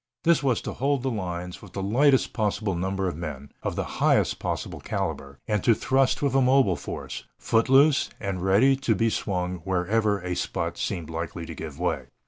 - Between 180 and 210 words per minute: Yes, average, 195 wpm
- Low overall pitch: Yes, low, 100 Hz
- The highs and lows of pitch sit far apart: Yes, wide, 6.4 semitones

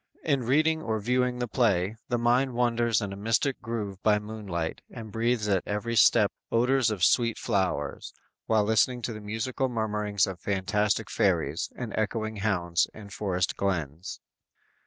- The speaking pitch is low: Yes, low, 110 Hz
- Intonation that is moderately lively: Yes, average, 3.0 semitones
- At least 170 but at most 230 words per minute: No, average, 155 wpm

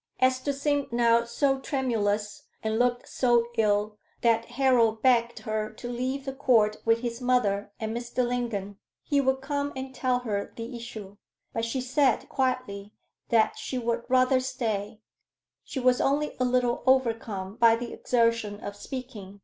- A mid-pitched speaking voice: No, high, 240 Hz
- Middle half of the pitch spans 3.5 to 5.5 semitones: No, average, 2.8 semitones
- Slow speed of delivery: No, average, 155 wpm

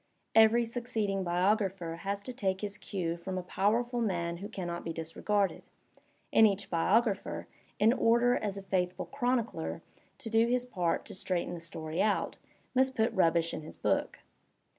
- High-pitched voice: Yes, high, 195 Hz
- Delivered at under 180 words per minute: Yes, average, 165 wpm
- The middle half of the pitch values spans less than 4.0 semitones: No, average, 4.6 semitones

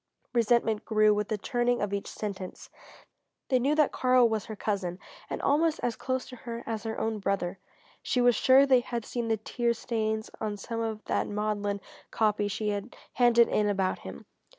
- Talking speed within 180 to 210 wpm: Yes, average, 190 wpm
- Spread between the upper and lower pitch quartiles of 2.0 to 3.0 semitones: Yes, average, 2.7 semitones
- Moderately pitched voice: No, high, 220 Hz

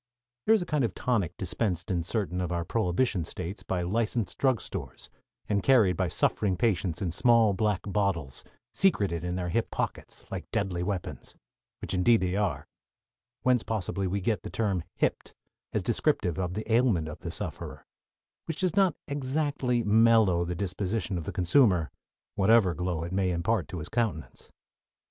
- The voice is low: Yes, low, 100 Hz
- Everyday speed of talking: Yes, average, 165 wpm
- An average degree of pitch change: Yes, average, 4.5 semitones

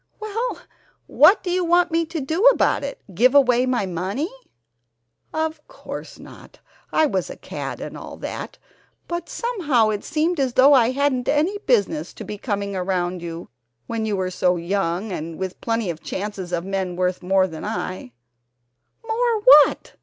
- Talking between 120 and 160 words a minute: No, average, 175 wpm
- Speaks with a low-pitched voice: No, high, 230 Hz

